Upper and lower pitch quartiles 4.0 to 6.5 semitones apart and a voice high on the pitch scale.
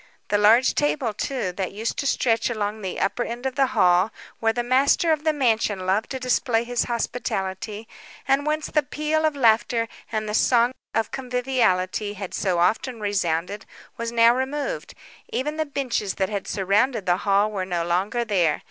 Yes: average, 4.5 semitones; high, 225 Hz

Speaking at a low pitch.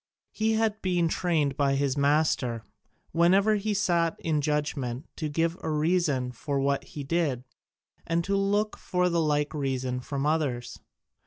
No: medium, 155 Hz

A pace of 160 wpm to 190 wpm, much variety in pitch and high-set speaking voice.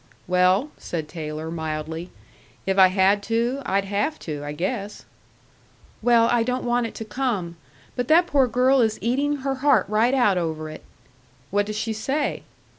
Yes: average, 170 wpm; wide, 5.7 semitones; high, 215 Hz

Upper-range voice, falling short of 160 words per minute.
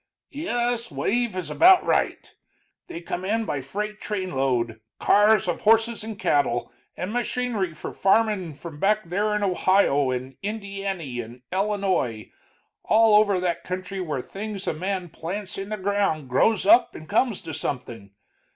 Yes: high, 195 Hz; average, 150 wpm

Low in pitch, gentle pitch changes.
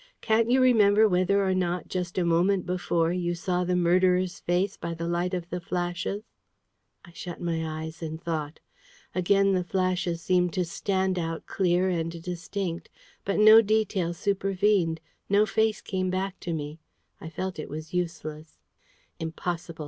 No: medium, 180 Hz; narrow, 2.3 semitones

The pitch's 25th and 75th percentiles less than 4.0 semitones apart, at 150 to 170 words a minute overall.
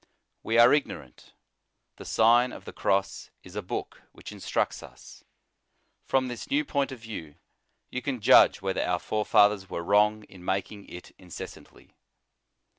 No: average, 4.3 semitones; average, 155 wpm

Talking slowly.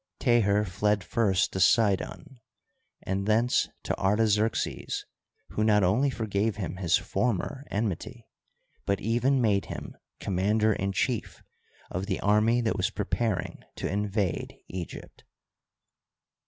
Yes: slow, 120 wpm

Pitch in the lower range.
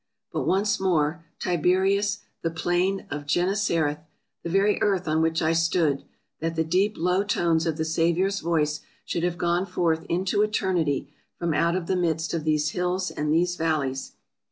No: medium, 170 Hz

